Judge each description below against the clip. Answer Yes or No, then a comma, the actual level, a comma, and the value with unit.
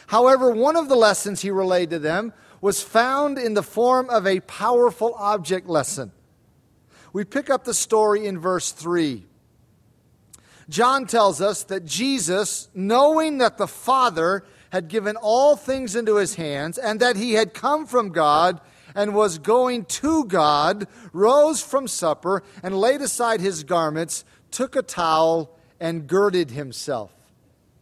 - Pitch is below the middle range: No, high, 200 Hz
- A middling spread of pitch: No, wide, 6.4 semitones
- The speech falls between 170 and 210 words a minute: No, average, 150 wpm